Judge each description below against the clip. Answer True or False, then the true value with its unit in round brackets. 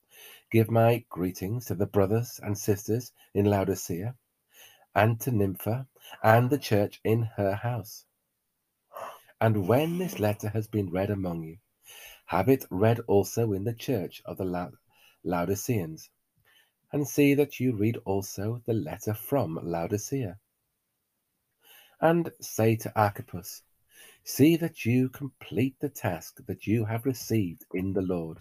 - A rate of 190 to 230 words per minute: False (140 wpm)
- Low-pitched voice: True (110 Hz)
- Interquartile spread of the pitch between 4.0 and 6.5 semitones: False (3.6 semitones)